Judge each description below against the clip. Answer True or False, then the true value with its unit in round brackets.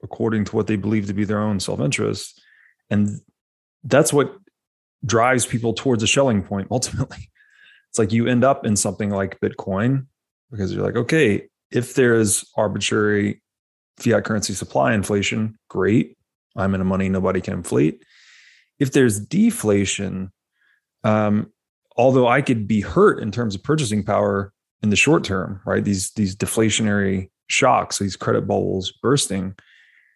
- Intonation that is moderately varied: True (3.2 semitones)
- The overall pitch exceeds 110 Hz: False (105 Hz)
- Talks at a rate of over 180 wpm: False (150 wpm)